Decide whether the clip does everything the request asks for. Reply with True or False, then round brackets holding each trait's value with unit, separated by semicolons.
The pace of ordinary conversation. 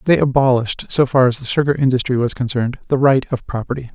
False (215 wpm)